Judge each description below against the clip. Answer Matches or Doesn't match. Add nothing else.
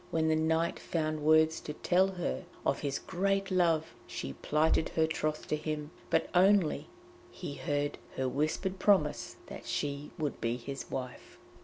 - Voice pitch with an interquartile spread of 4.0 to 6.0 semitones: Doesn't match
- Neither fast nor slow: Matches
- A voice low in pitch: Doesn't match